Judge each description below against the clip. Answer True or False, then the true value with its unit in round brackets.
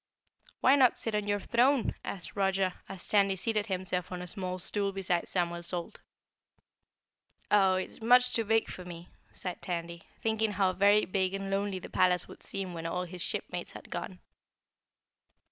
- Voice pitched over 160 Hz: True (190 Hz)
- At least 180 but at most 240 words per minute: False (170 wpm)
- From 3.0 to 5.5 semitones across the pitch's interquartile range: False (2.5 semitones)